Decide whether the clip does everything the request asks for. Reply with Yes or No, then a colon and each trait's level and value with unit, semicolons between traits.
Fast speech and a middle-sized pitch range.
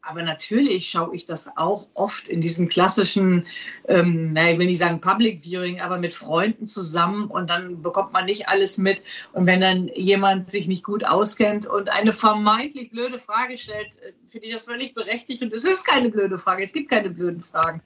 Yes: fast, 200 wpm; average, 3.5 semitones